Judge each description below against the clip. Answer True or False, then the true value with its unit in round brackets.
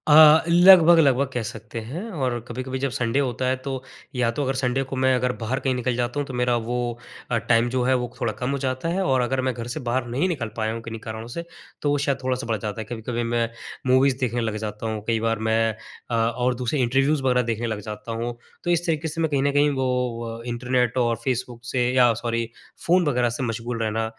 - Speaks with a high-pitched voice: False (125 Hz)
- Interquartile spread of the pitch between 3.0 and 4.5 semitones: False (2.5 semitones)